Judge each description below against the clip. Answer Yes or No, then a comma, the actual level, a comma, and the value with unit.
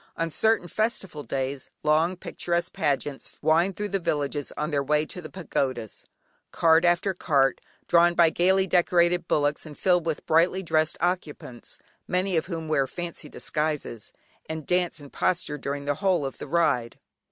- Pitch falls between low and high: Yes, medium, 160 Hz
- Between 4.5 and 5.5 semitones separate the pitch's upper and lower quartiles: No, average, 3.4 semitones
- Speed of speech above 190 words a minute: No, average, 165 wpm